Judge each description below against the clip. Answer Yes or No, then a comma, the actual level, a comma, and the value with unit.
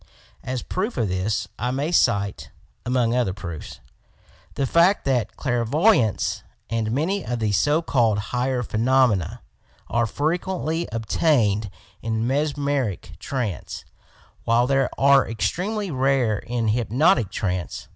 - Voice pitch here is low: Yes, low, 125 Hz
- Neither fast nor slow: No, slow, 120 wpm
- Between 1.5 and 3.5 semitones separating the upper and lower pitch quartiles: No, average, 4.7 semitones